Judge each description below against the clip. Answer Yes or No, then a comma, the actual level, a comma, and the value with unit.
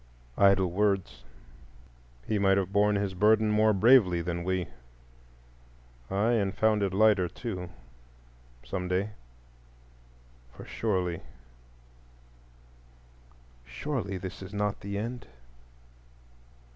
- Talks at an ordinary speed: No, slow, 95 wpm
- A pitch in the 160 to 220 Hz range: No, very low, 95 Hz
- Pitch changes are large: No, average, 3.4 semitones